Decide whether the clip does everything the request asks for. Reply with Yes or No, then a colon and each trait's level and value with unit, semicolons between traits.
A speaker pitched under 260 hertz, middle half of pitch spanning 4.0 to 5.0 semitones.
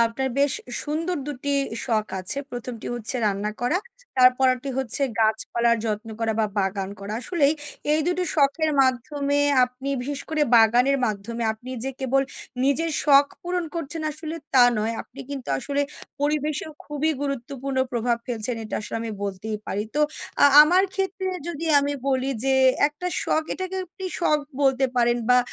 No: very high, 270 Hz; average, 4.4 semitones